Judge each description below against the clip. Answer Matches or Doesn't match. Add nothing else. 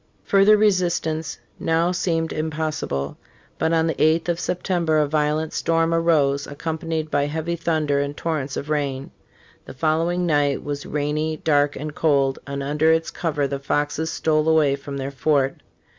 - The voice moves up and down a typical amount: Doesn't match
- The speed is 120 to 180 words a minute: Matches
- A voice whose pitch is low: Doesn't match